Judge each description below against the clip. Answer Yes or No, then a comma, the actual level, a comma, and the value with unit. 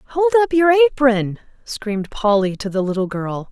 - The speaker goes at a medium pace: Yes, average, 170 wpm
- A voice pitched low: No, high, 245 Hz